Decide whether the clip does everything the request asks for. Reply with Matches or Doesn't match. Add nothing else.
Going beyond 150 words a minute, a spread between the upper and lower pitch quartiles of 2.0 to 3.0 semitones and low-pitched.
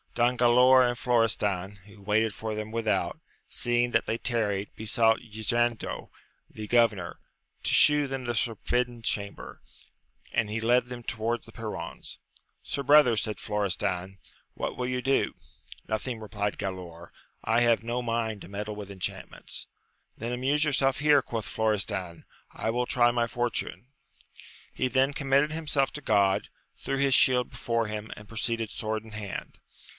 Matches